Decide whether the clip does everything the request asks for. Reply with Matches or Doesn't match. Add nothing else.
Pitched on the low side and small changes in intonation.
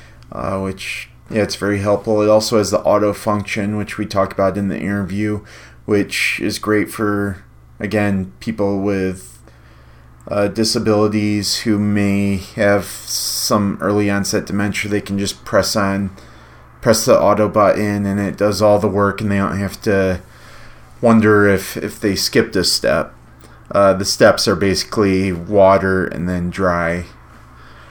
Matches